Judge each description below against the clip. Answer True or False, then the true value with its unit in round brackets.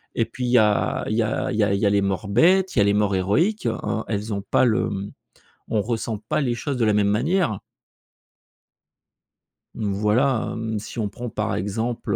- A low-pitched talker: True (110 Hz)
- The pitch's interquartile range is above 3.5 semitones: False (2.9 semitones)